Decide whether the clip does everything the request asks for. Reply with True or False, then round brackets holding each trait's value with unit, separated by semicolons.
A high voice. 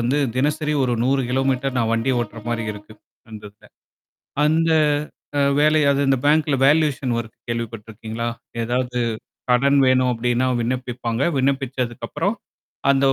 False (125 Hz)